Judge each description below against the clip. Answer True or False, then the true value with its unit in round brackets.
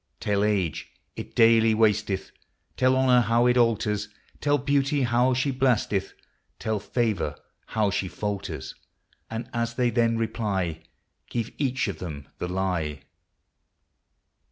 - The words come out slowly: True (130 wpm)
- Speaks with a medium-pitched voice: False (115 Hz)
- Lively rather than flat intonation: False (3.7 semitones)